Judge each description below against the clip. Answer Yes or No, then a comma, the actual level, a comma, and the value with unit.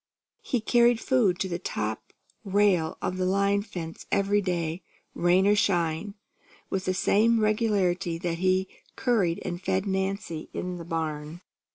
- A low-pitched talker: No, high, 190 Hz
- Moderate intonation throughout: Yes, average, 3.0 semitones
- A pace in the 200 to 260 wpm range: No, average, 150 wpm